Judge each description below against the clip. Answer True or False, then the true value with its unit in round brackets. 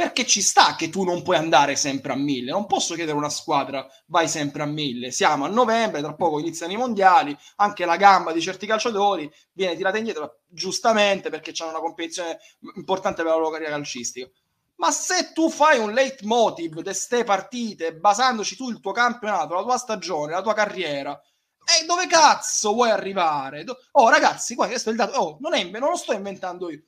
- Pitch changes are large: True (6.6 semitones)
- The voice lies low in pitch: False (190 Hz)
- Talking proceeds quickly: True (195 wpm)